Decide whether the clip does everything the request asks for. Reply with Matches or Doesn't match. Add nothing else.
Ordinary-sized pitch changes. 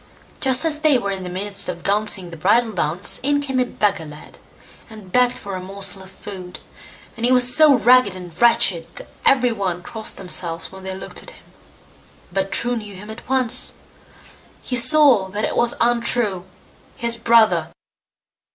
Matches